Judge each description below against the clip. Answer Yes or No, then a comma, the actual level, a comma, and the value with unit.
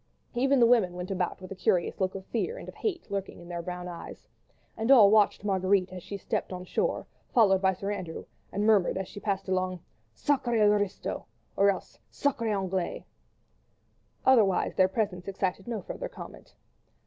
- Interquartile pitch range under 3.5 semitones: Yes, average, 3.1 semitones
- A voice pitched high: Yes, high, 195 Hz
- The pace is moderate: Yes, average, 180 wpm